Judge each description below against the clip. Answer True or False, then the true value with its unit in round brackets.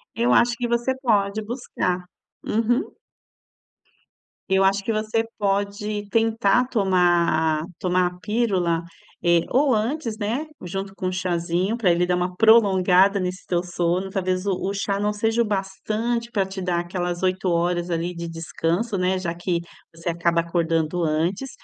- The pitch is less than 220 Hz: True (190 Hz)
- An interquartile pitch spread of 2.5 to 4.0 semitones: True (3.6 semitones)